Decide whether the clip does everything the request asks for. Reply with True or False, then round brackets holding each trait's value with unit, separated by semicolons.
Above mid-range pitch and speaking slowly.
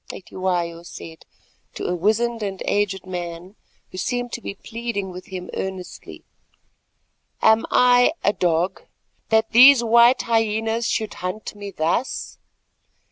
True (205 Hz; 130 wpm)